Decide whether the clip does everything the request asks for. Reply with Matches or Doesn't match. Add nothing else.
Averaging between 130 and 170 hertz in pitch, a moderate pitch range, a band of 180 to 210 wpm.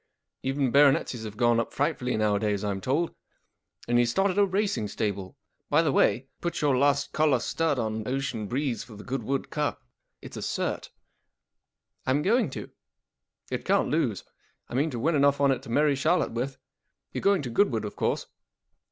Matches